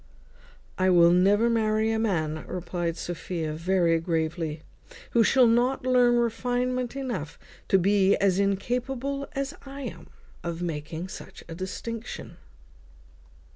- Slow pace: Yes, slow, 130 wpm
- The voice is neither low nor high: No, high, 200 Hz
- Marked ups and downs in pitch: Yes, wide, 6.1 semitones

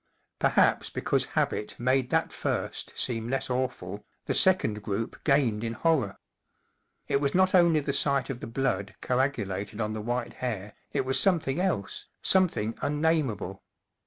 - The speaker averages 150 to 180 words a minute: Yes, average, 155 wpm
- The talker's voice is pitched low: Yes, low, 125 Hz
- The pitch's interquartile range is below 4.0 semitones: No, average, 5.1 semitones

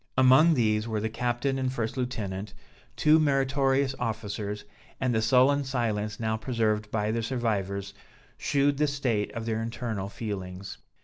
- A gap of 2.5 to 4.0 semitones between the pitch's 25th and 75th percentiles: Yes, average, 3.7 semitones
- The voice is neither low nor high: No, low, 115 Hz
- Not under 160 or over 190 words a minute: No, average, 145 wpm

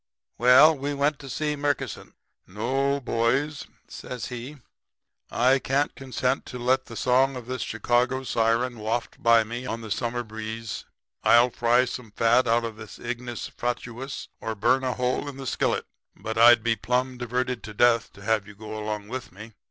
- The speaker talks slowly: No, average, 180 wpm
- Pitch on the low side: Yes, low, 120 Hz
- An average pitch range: No, narrow, 2.3 semitones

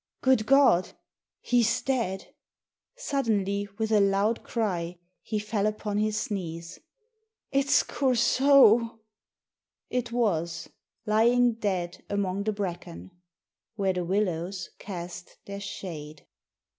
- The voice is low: No, high, 205 Hz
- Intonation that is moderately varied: Yes, average, 4.2 semitones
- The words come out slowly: Yes, slow, 105 wpm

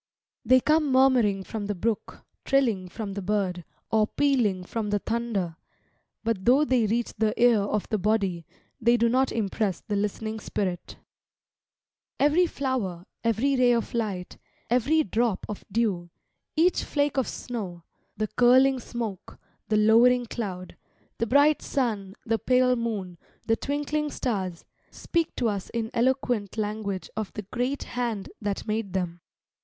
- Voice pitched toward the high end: Yes, high, 225 Hz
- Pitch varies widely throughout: No, average, 3.9 semitones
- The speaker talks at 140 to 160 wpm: Yes, average, 150 wpm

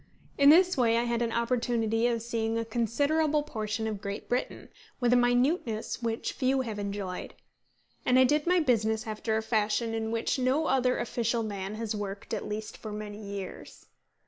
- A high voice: Yes, high, 230 Hz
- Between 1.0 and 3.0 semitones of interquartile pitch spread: Yes, average, 2.7 semitones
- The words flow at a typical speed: Yes, average, 180 wpm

